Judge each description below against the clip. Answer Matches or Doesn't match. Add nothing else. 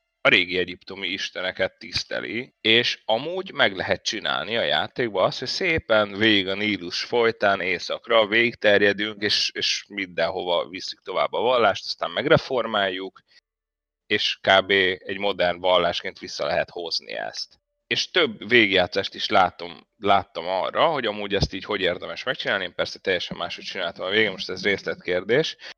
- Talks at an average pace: Matches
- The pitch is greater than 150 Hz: Doesn't match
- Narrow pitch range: Doesn't match